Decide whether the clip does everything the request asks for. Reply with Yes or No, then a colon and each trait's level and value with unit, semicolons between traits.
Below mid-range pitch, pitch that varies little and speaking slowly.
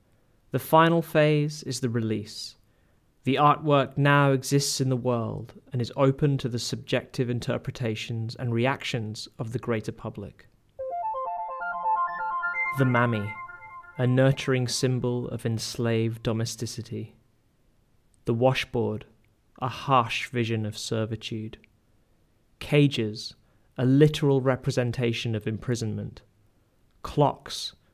No: low, 120 Hz; average, 3.5 semitones; slow, 105 wpm